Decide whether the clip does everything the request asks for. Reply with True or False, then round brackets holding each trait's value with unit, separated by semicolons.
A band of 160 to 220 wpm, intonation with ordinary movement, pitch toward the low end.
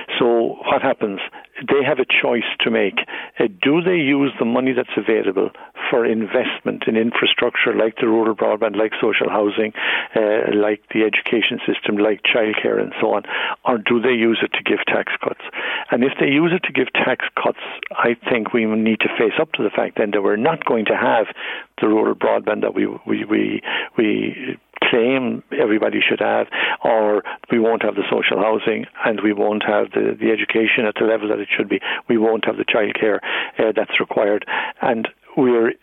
False (200 wpm; 1.9 semitones; 110 Hz)